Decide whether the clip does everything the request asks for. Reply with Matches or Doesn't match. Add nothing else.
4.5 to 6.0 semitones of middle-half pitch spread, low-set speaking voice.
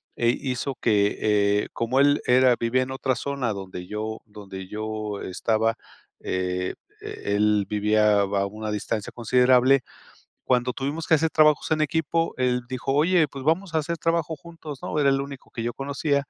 Matches